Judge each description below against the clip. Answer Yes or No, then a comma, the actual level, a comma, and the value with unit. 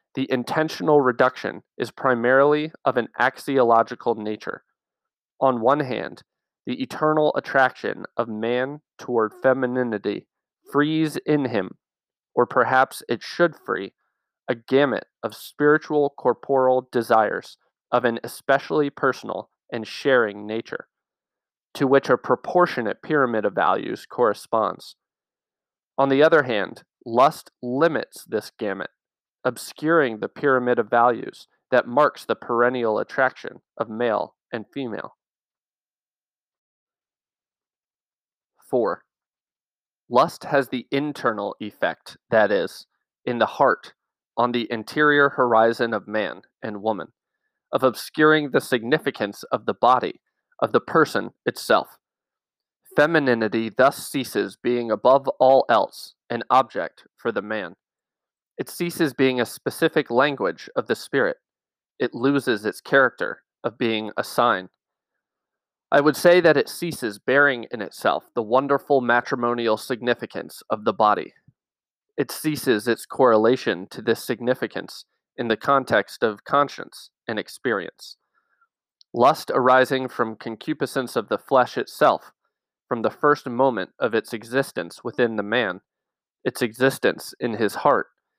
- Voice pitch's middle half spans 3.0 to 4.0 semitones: Yes, average, 3.5 semitones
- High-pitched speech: No, low, 130 Hz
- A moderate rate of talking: No, slow, 125 wpm